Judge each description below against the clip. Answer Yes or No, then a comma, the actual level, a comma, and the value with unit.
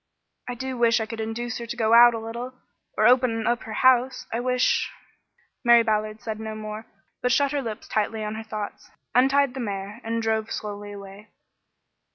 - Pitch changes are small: Yes, narrow, 2.1 semitones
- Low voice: No, high, 225 Hz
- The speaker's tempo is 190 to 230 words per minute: Yes, average, 200 wpm